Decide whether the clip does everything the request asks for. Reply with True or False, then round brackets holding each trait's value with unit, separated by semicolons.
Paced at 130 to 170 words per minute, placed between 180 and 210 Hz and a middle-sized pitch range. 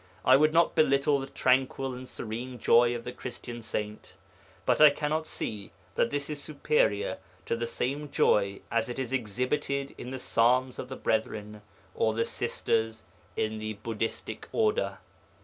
False (165 wpm; 125 Hz; 3.8 semitones)